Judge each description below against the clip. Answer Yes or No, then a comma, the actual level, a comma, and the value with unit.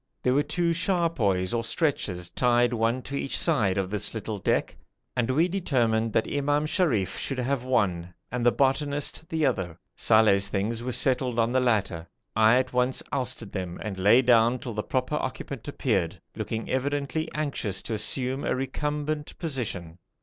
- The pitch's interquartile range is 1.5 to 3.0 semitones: No, average, 4.7 semitones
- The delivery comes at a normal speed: Yes, average, 170 wpm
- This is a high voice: No, low, 125 Hz